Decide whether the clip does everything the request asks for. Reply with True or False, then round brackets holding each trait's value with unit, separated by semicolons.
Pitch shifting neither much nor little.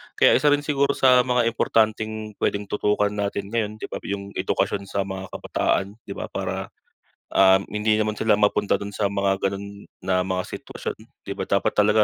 False (1.8 semitones)